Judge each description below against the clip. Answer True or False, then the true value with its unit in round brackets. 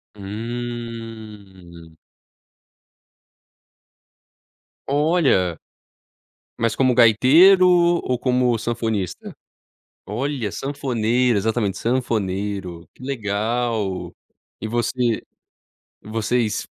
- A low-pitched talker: True (115 Hz)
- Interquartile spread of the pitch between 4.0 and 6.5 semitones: False (3.5 semitones)